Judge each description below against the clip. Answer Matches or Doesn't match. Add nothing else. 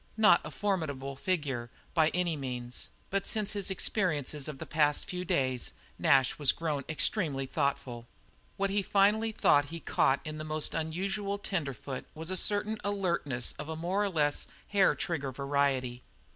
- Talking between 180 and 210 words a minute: Doesn't match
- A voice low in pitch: Doesn't match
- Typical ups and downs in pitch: Doesn't match